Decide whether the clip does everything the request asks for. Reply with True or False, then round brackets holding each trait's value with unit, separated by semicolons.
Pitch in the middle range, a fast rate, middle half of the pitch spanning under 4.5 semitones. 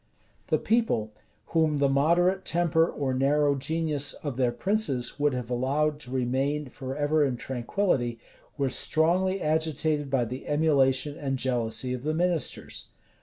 False (145 Hz; 140 wpm; 3.4 semitones)